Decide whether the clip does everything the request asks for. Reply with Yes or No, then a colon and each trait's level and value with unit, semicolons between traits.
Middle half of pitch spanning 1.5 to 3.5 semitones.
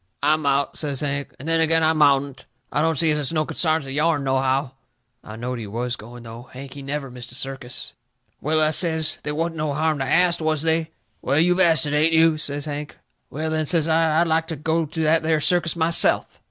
Yes: average, 2.8 semitones